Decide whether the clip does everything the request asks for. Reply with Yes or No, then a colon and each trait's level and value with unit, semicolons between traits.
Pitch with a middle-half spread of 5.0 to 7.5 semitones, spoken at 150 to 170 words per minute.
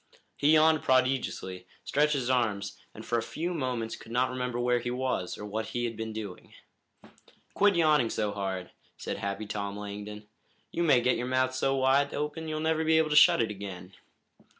No: average, 5.3 semitones; average, 195 wpm